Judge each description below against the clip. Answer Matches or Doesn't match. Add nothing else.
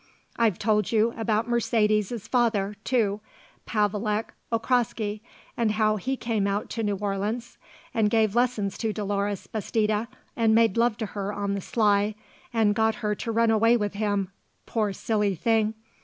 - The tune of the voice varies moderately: Doesn't match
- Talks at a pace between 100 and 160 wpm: Matches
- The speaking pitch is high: Matches